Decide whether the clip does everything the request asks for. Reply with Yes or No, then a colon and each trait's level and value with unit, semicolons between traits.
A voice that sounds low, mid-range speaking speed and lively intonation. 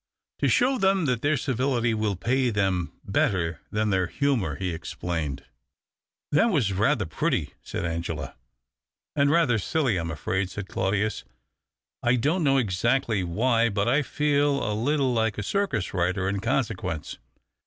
Yes: low, 110 Hz; average, 160 wpm; wide, 6.5 semitones